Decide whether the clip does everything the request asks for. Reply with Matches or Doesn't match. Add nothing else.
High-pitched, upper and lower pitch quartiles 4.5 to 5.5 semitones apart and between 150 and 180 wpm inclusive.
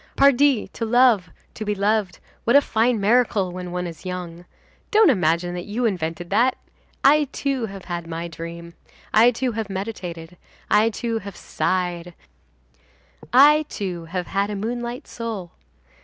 Matches